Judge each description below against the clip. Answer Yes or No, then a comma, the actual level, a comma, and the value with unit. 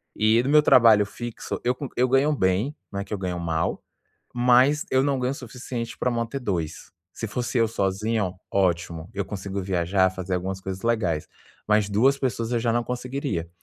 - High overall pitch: No, low, 110 Hz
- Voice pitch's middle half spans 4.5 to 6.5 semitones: Yes, average, 4.8 semitones